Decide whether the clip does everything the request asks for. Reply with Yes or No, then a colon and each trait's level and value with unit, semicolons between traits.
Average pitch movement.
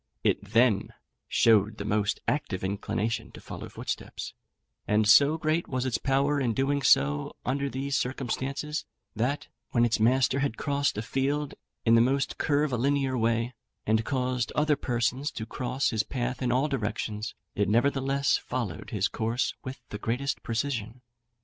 Yes: average, 3.8 semitones